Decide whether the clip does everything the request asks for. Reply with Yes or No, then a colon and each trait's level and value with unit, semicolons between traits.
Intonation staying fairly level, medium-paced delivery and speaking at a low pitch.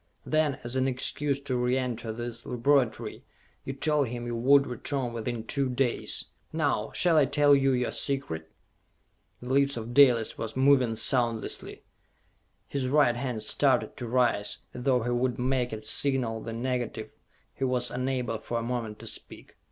Yes: narrow, 2.3 semitones; average, 165 wpm; low, 125 Hz